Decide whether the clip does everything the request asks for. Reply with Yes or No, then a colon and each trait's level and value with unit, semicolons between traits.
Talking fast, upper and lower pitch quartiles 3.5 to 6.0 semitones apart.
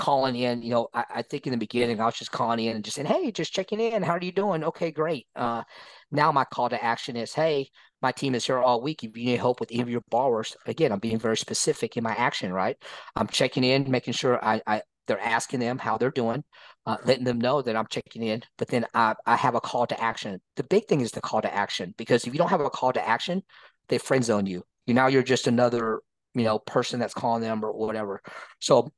No: fast, 260 wpm; average, 3.1 semitones